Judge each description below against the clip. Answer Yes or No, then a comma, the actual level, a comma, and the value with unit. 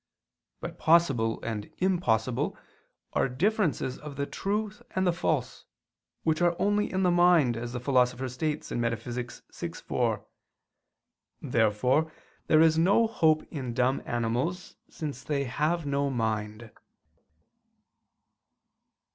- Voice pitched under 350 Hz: Yes, medium, 140 Hz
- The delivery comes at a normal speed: No, slow, 120 wpm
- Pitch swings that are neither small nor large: No, wide, 6.1 semitones